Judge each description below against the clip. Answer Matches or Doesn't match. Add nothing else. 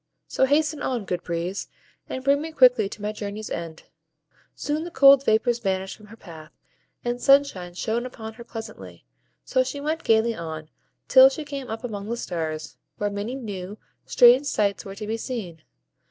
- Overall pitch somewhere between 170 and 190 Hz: Doesn't match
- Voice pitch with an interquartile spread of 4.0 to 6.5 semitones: Matches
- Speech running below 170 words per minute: Doesn't match